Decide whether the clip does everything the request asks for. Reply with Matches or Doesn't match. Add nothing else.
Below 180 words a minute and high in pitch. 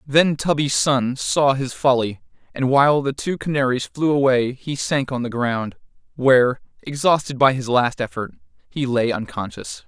Doesn't match